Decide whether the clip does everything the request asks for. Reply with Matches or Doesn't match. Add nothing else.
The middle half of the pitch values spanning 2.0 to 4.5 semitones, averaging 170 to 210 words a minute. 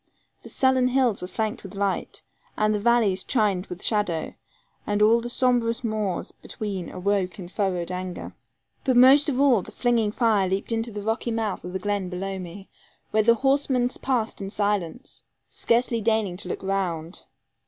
Matches